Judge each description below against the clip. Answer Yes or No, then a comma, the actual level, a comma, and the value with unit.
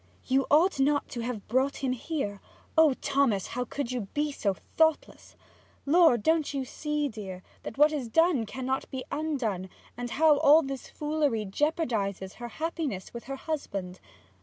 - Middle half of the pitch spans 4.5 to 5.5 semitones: Yes, average, 4.8 semitones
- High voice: Yes, very high, 270 Hz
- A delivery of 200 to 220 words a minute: No, average, 160 wpm